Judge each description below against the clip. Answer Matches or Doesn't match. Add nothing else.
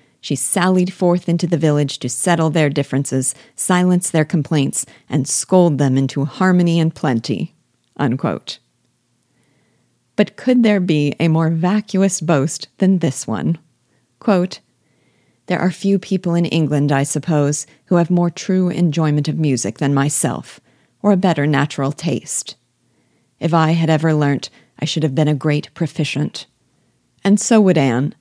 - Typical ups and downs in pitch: Matches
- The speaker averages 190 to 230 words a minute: Doesn't match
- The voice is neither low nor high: Matches